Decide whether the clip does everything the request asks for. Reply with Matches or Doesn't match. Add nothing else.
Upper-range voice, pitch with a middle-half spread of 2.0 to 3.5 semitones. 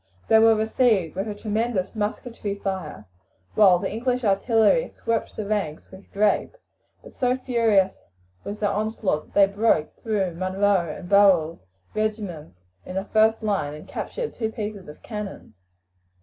Matches